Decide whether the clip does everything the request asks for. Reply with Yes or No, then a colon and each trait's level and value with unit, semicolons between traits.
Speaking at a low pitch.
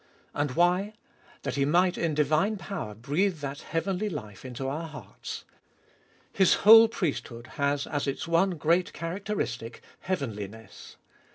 No: medium, 155 Hz